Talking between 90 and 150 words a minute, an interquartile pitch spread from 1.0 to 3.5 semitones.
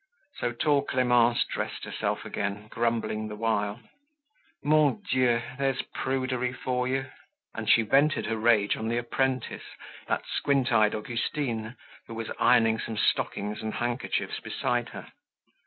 Yes: average, 140 wpm; average, 2.7 semitones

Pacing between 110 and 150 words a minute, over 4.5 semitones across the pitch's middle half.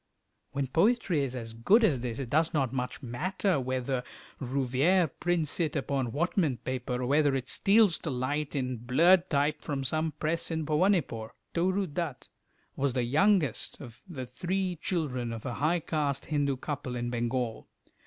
No: average, 165 wpm; average, 4.9 semitones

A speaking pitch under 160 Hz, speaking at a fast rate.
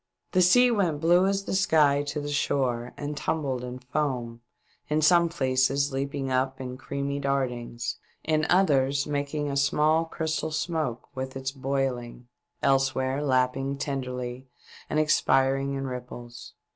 No: medium, 140 Hz; average, 145 wpm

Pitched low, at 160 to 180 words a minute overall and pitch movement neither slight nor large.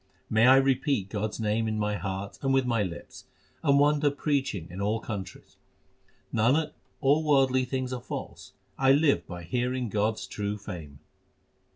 Yes: low, 120 Hz; average, 170 wpm; average, 4.6 semitones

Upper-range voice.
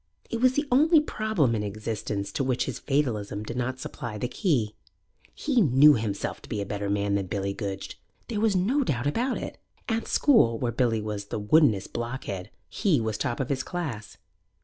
No: low, 120 Hz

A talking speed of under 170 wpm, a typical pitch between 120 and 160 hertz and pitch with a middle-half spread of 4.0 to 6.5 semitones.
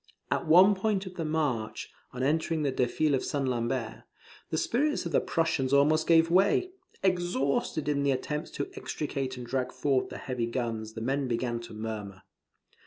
No: average, 175 wpm; medium, 140 Hz; average, 4.7 semitones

